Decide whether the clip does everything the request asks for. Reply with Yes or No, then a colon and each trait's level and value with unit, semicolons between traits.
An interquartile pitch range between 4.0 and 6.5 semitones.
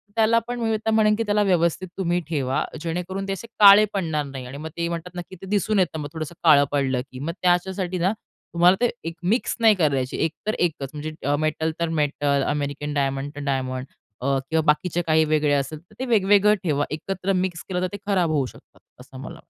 Yes: average, 4.8 semitones